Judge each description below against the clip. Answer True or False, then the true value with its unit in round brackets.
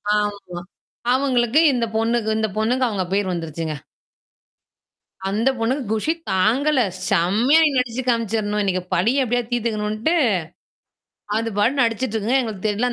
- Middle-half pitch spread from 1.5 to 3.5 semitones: True (3.2 semitones)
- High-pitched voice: True (225 Hz)